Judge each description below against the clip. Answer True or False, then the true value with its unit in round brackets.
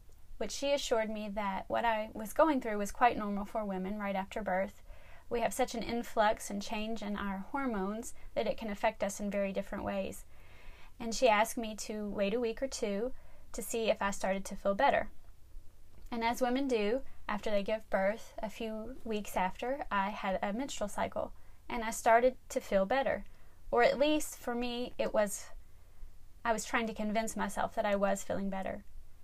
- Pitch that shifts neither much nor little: True (3.2 semitones)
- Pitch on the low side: False (215 Hz)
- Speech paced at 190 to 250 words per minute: True (195 wpm)